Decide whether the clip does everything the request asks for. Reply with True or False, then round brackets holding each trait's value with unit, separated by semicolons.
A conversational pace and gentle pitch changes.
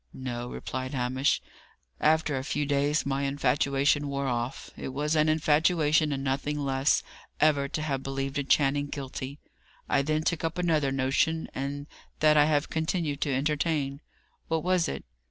True (160 wpm; 2.1 semitones)